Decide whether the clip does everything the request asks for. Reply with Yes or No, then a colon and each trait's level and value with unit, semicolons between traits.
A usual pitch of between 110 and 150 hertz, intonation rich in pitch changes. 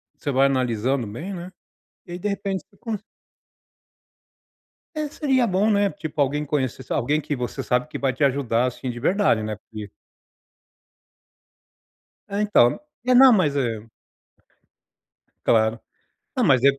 Yes: medium, 140 Hz; wide, 8.3 semitones